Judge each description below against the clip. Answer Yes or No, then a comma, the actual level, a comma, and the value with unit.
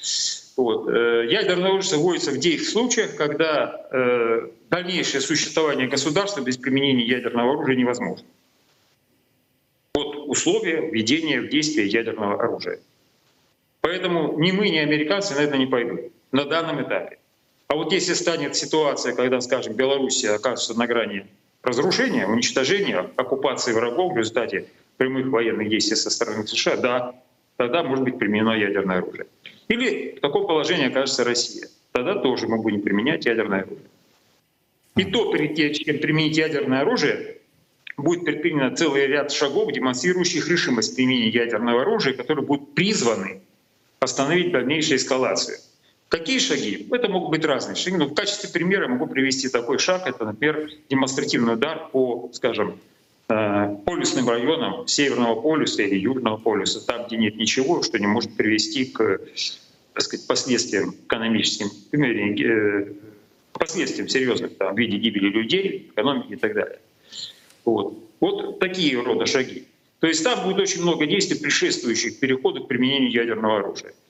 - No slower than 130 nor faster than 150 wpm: Yes, average, 140 wpm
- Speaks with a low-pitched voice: Yes, low, 130 Hz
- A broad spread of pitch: Yes, wide, 7.1 semitones